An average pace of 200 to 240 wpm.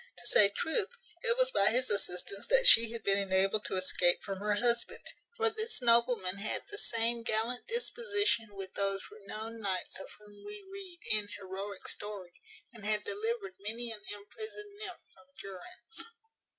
No: average, 165 wpm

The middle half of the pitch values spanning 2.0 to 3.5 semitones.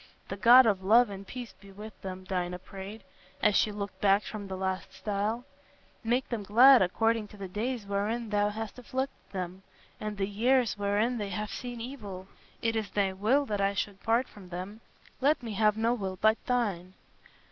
Yes: average, 2.9 semitones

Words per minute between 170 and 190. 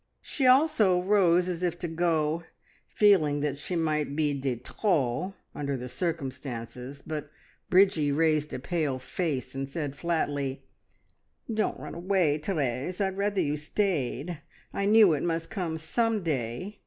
No: average, 145 wpm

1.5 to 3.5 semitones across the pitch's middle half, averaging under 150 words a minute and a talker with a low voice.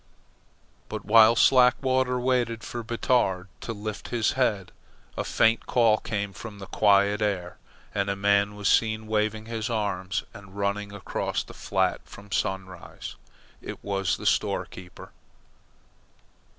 Yes: narrow, 2.5 semitones; slow, 135 wpm; low, 105 Hz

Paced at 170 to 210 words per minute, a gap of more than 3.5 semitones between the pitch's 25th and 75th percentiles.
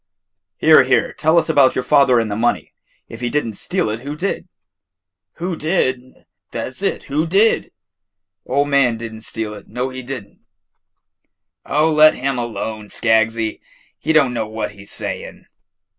Yes: average, 175 wpm; average, 5.1 semitones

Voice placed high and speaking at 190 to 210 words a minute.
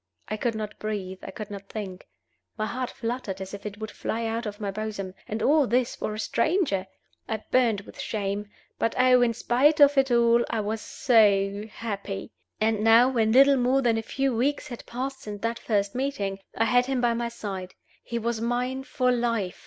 Yes: high, 225 Hz; fast, 205 wpm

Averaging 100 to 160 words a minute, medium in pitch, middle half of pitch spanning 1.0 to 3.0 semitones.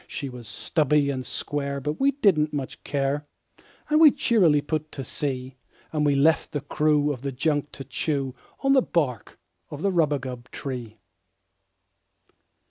Yes: average, 150 wpm; medium, 145 Hz; narrow, 2.5 semitones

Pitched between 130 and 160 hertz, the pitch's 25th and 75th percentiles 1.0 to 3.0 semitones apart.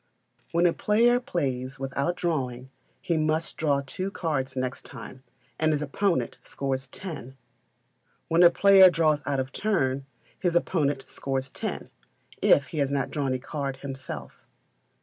No: medium, 140 Hz; average, 4.3 semitones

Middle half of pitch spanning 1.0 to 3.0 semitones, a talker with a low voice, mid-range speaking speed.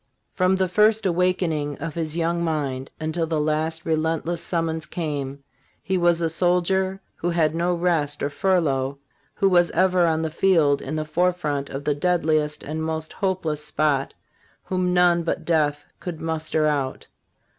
No: average, 2.7 semitones; medium, 160 Hz; average, 160 wpm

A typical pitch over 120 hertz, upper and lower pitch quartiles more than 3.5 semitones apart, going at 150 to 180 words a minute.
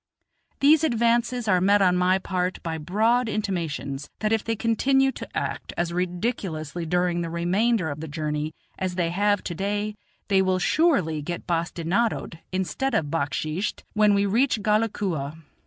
Yes: medium, 185 Hz; average, 4.5 semitones; average, 160 wpm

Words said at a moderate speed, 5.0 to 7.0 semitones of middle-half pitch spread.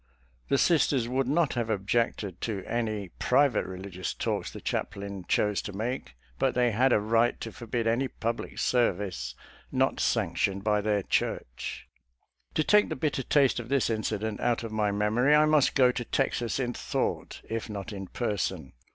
No: average, 170 wpm; average, 3.7 semitones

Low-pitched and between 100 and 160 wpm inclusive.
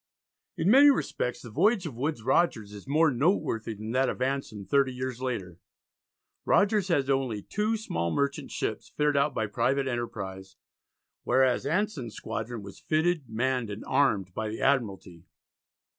Yes: low, 130 Hz; average, 155 wpm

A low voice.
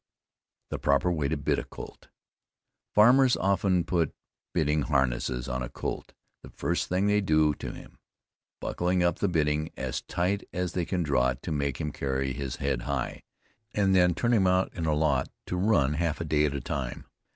Yes: very low, 80 Hz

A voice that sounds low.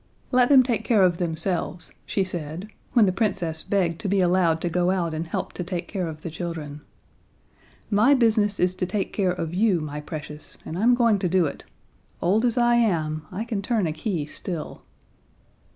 No: medium, 185 Hz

